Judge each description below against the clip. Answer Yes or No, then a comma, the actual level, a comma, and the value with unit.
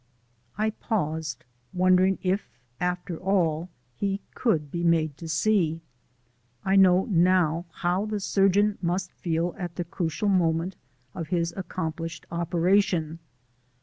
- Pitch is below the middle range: No, medium, 180 Hz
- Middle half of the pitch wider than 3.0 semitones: No, average, 2.7 semitones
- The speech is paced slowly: Yes, slow, 120 wpm